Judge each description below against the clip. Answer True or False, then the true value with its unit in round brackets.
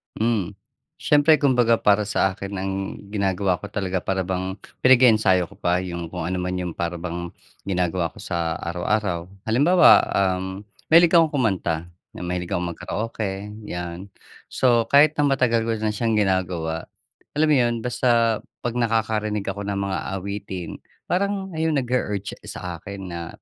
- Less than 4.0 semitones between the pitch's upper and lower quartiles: False (4.5 semitones)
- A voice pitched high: False (100 Hz)